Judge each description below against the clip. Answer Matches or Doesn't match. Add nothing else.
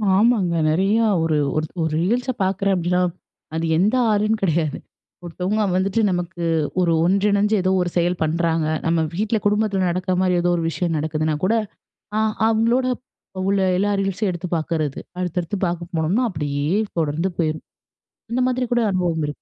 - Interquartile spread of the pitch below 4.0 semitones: Matches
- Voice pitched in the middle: Matches